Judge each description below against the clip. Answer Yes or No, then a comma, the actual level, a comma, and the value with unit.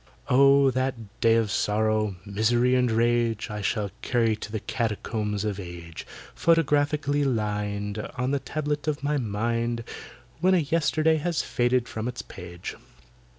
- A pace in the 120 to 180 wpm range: Yes, average, 145 wpm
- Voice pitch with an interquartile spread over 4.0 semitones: Yes, average, 4.8 semitones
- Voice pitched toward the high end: No, low, 120 Hz